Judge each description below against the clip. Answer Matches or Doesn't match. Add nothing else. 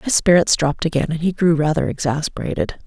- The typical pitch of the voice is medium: Matches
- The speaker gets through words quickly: Doesn't match